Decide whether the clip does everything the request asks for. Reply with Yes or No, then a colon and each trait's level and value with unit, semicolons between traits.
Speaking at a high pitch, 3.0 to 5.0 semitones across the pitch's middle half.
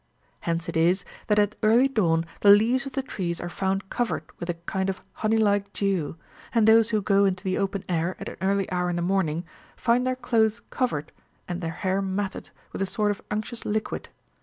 Yes: high, 195 Hz; average, 3.3 semitones